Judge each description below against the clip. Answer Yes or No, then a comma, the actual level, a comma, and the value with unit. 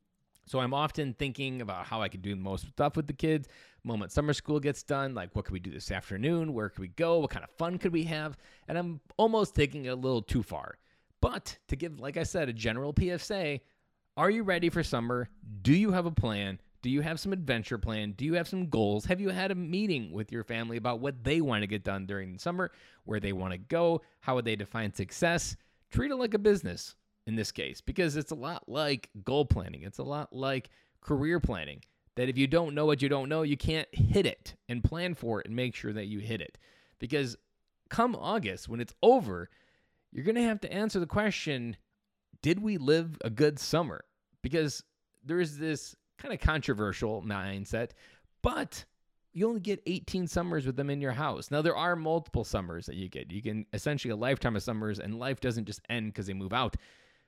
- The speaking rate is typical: No, fast, 225 wpm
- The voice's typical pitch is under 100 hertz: No, low, 135 Hz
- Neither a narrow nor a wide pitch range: No, wide, 7.4 semitones